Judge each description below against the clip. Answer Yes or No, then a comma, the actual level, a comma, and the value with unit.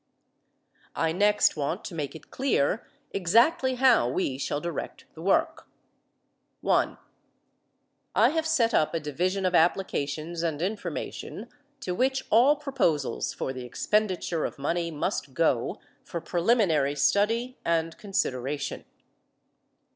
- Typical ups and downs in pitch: No, wide, 6.5 semitones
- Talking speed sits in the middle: No, slow, 125 wpm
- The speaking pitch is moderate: Yes, medium, 175 Hz